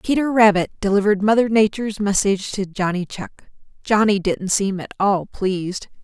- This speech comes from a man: No, female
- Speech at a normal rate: Yes, average, 150 wpm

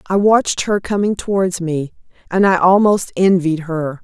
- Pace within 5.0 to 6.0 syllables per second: No, 4.6 syllables/s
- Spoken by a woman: Yes, female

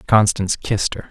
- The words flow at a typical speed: Yes, average, 165 wpm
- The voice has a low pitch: Yes, low, 105 Hz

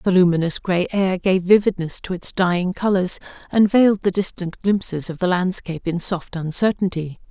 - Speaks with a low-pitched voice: No, medium, 185 Hz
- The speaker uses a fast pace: No, average, 175 wpm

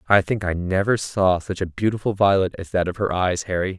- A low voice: Yes, very low, 95 Hz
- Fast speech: Yes, fast, 240 wpm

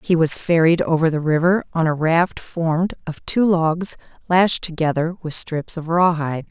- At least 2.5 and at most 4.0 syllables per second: No, 4.6 syllables/s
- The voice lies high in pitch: No, medium, 165 Hz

